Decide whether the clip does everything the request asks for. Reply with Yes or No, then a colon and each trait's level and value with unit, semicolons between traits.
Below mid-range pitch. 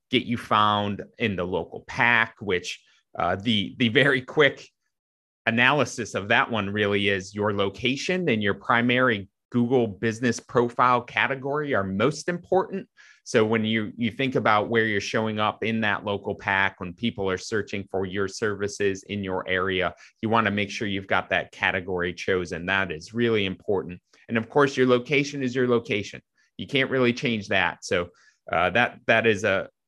Yes: low, 110 Hz